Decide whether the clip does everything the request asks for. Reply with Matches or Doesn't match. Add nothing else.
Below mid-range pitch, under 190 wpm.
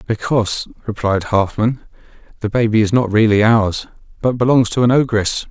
Matches